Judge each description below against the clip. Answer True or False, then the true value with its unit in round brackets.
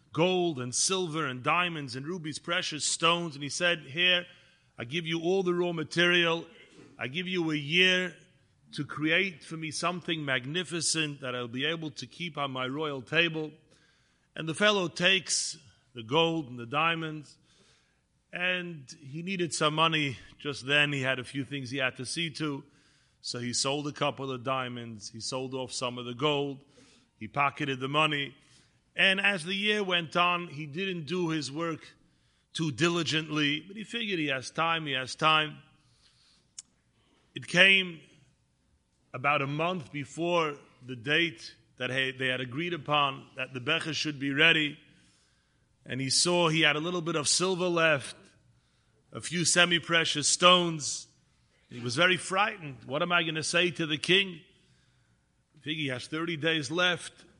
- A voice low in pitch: False (155 Hz)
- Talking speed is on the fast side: False (170 wpm)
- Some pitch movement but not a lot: True (4.0 semitones)